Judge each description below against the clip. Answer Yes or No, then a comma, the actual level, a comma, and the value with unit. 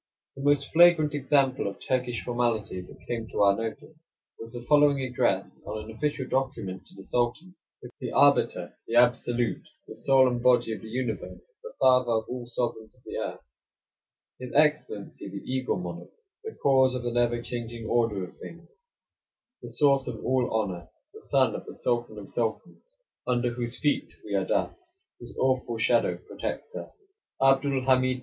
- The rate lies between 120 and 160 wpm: No, average, 180 wpm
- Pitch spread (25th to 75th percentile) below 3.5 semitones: Yes, average, 2.9 semitones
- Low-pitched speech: Yes, low, 125 Hz